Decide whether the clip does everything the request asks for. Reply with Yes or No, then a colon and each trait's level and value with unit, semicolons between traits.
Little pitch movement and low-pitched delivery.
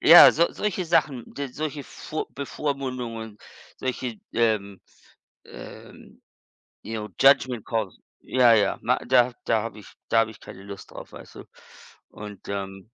No: average, 4.5 semitones; low, 115 Hz